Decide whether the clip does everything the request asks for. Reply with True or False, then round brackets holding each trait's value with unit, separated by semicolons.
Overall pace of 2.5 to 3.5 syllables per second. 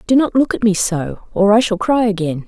False (5.5 syllables/s)